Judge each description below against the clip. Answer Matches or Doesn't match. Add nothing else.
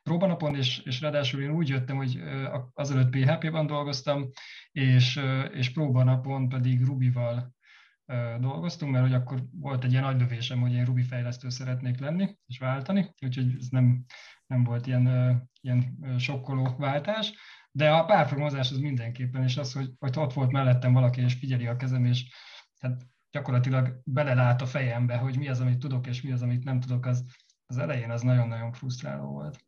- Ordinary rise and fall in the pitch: Doesn't match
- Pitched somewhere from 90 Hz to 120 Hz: Doesn't match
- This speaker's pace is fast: Matches